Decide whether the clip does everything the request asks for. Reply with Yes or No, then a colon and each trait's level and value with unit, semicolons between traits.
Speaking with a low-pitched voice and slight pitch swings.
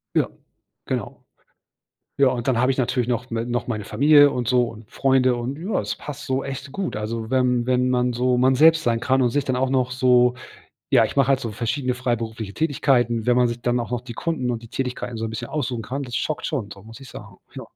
Yes: low, 125 Hz; narrow, 2.0 semitones